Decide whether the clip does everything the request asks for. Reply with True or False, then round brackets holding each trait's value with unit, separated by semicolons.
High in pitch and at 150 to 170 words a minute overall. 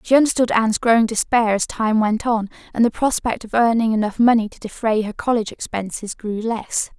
False (225 Hz; 200 wpm)